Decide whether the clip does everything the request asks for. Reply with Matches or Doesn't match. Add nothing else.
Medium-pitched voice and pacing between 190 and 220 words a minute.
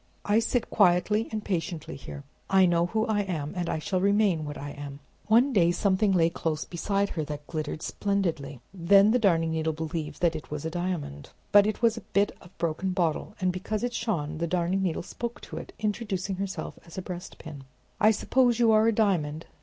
Matches